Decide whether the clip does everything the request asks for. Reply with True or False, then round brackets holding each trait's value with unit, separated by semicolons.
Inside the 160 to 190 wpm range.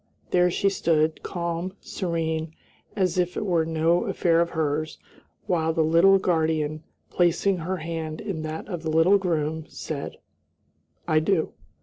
False (145 wpm)